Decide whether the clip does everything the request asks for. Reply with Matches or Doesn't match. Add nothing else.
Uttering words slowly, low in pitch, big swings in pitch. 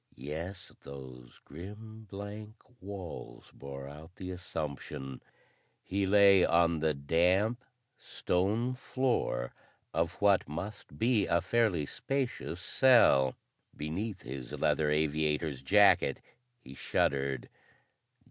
Matches